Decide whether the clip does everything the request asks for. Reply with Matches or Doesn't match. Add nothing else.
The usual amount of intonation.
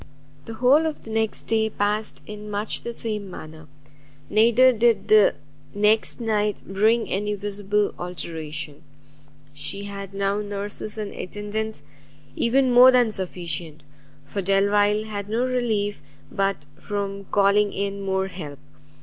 Doesn't match